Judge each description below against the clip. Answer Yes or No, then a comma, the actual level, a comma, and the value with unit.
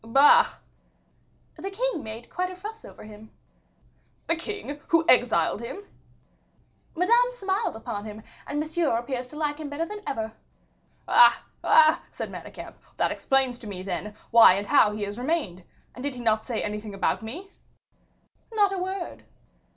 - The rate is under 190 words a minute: Yes, average, 160 wpm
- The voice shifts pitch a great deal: Yes, wide, 8.7 semitones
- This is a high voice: Yes, very high, 275 Hz